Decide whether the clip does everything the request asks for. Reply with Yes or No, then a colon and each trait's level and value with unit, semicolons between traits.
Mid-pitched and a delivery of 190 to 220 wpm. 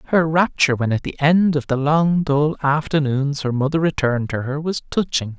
Yes: medium, 145 Hz; average, 200 wpm